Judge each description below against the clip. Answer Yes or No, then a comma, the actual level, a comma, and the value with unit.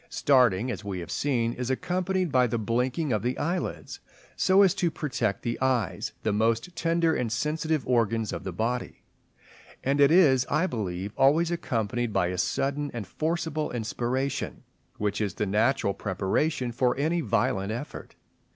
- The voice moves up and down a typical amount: No, wide, 5.7 semitones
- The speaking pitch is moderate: No, low, 125 Hz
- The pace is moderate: Yes, average, 160 wpm